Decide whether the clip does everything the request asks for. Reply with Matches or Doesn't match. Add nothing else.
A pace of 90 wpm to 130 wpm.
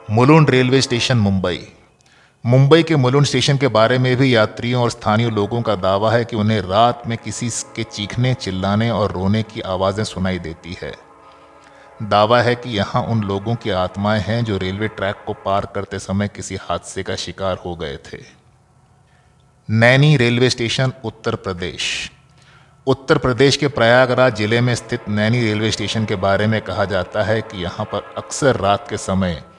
Doesn't match